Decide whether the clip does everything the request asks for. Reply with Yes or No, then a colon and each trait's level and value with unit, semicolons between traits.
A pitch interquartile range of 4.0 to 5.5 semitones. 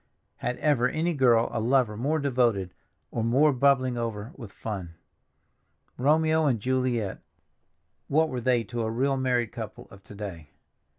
No: average, 3.6 semitones